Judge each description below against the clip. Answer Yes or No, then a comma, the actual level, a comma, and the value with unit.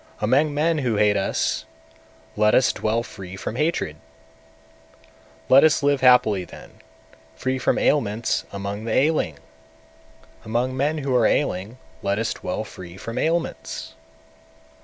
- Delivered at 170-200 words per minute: No, average, 140 wpm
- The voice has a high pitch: No, low, 115 Hz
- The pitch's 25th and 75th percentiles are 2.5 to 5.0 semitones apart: No, wide, 5.5 semitones